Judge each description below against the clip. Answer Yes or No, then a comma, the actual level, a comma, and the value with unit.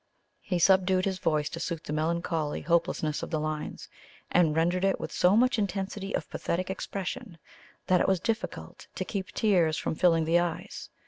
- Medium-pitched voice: Yes, medium, 175 Hz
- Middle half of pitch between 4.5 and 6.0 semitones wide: No, average, 2.8 semitones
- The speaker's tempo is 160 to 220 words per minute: Yes, average, 180 wpm